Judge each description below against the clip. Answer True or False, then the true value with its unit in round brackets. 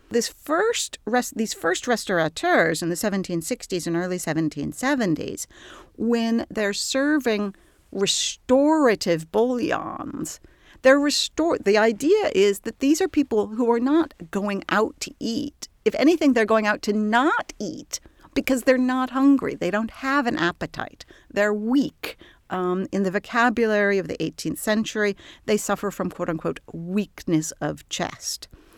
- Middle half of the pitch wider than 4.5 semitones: True (5.3 semitones)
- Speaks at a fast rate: False (140 wpm)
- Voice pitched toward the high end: True (220 Hz)